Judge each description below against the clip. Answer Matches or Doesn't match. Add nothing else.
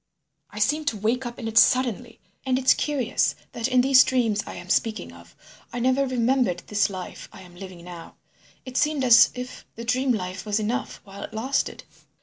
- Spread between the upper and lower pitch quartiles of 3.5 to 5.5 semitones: Matches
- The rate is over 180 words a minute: Matches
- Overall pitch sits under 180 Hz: Doesn't match